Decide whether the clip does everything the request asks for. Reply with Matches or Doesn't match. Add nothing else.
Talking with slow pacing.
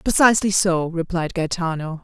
Matches